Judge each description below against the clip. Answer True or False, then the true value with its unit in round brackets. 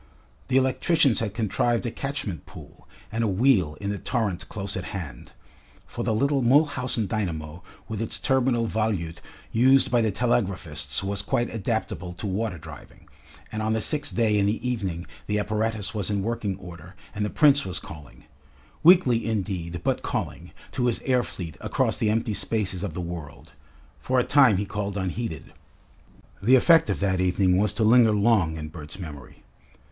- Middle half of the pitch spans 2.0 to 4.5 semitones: True (4.2 semitones)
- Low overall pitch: True (105 Hz)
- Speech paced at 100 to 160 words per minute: False (175 wpm)